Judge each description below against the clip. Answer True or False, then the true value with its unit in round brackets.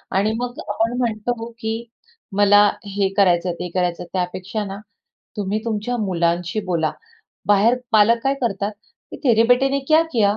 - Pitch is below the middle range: False (210 Hz)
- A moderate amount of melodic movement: True (3.4 semitones)